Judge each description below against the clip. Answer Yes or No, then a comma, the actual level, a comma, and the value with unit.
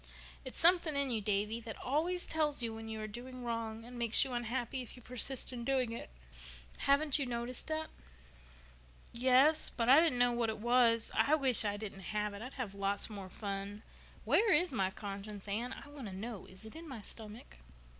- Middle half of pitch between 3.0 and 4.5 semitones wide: Yes, average, 3.9 semitones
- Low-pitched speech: No, high, 235 Hz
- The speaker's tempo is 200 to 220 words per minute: Yes, fast, 205 wpm